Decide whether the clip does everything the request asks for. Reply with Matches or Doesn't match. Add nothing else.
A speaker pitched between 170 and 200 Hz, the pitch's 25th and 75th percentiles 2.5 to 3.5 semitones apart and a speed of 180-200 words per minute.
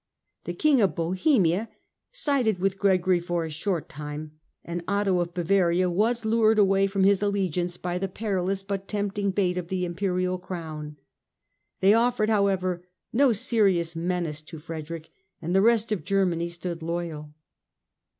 Doesn't match